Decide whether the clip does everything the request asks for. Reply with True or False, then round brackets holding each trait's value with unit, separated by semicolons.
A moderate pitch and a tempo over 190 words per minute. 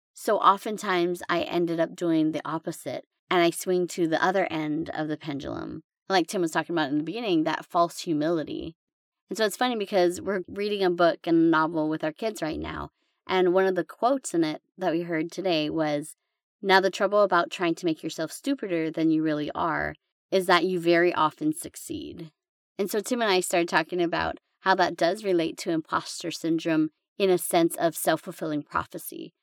True (175 Hz; 200 wpm)